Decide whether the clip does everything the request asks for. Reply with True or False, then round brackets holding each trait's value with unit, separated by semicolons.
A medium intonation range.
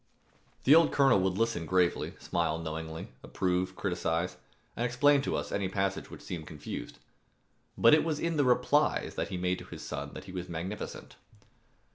False (6.3 semitones)